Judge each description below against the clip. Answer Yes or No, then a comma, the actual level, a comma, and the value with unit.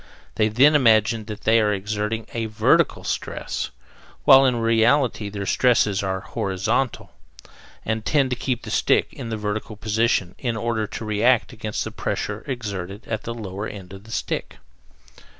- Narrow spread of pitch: Yes, narrow, 2.1 semitones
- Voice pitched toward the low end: Yes, low, 110 Hz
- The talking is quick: No, average, 165 wpm